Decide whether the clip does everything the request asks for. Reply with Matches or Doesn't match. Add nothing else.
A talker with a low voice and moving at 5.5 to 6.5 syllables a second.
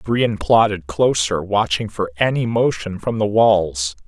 Doesn't match